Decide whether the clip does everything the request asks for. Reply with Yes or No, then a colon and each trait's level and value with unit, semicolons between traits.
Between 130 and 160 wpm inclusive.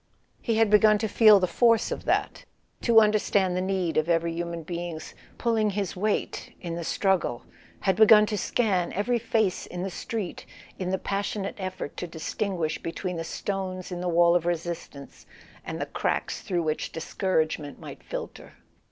No: average, 170 wpm